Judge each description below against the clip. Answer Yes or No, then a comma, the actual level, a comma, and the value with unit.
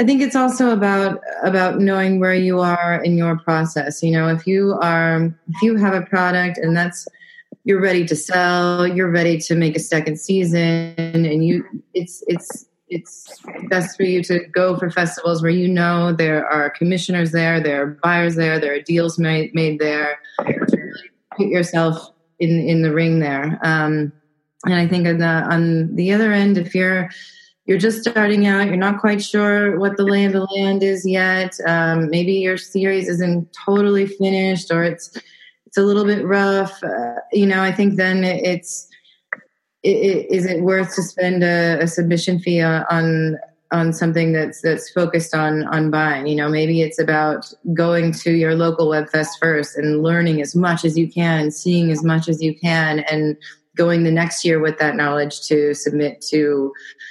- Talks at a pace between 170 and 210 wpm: Yes, average, 185 wpm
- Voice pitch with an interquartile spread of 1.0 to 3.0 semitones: Yes, average, 2.7 semitones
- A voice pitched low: No, medium, 170 Hz